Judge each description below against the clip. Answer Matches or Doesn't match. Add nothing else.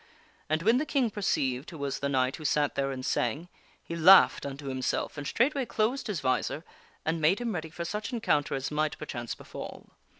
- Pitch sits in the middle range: Matches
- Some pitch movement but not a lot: Doesn't match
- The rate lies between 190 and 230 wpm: Matches